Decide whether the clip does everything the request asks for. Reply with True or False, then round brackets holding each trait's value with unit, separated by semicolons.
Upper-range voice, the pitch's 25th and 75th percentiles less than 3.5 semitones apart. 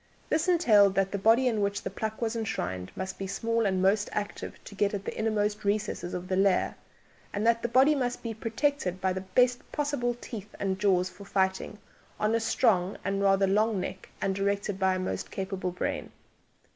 True (200 Hz; 3.0 semitones)